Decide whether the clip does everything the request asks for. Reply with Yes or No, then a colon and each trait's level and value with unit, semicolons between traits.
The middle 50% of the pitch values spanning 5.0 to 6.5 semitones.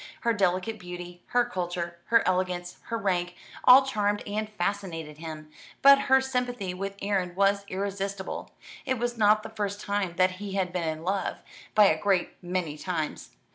No: average, 3.1 semitones